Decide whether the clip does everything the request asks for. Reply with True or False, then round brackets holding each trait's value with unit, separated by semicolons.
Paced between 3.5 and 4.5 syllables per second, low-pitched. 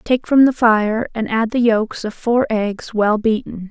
False (4.0 syllables/s; 225 Hz)